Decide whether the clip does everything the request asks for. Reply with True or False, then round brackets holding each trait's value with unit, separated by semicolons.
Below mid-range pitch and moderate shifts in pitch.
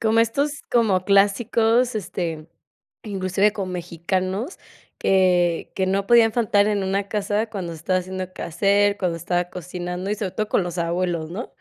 False (195 Hz; 3.0 semitones)